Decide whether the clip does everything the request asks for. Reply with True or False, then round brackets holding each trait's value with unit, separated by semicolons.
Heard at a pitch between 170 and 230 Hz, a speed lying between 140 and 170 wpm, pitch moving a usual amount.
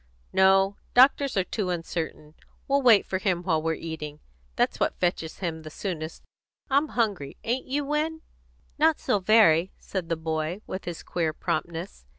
False (185 Hz; 165 wpm; 5.8 semitones)